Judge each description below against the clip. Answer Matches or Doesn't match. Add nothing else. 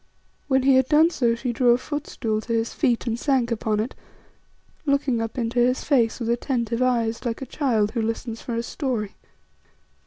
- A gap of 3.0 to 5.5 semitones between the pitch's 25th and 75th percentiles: Doesn't match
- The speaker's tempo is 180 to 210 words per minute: Matches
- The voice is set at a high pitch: Matches